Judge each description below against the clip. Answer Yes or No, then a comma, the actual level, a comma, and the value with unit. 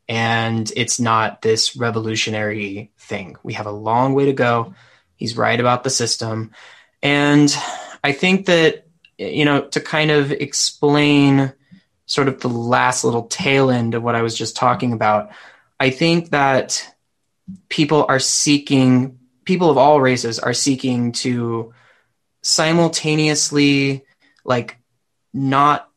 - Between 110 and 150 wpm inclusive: Yes, slow, 135 wpm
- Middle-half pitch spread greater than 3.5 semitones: Yes, average, 3.9 semitones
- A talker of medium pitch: No, low, 130 Hz